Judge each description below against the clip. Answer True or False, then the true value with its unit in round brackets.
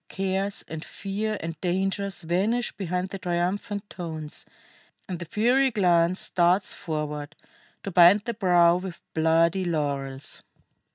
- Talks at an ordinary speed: False (125 wpm)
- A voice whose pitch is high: False (180 Hz)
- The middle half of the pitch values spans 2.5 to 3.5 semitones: True (3.0 semitones)